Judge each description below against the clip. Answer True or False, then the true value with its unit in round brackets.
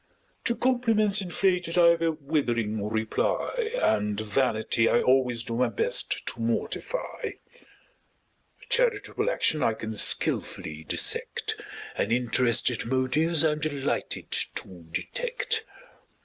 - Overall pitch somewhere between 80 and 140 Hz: True (135 Hz)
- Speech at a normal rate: False (110 wpm)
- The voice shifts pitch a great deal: True (8.7 semitones)